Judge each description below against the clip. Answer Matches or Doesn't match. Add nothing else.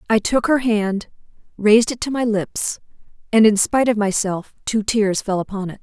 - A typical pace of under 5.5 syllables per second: Matches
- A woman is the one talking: Matches